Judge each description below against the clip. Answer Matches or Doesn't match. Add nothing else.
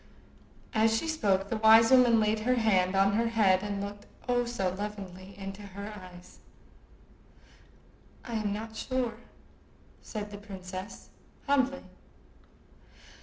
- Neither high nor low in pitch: Doesn't match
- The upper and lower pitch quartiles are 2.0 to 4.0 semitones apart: Matches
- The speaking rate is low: Matches